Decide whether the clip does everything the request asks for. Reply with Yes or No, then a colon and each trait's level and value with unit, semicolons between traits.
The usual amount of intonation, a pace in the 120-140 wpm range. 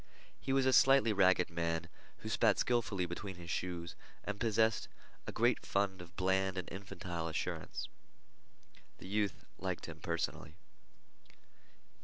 Yes: average, 3.7 semitones; slow, 135 wpm